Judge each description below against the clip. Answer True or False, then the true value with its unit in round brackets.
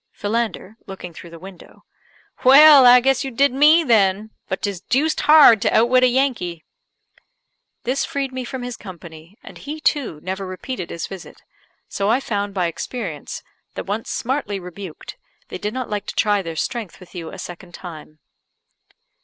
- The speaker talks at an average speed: True (175 wpm)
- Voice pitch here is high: True (210 Hz)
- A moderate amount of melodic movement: False (5.9 semitones)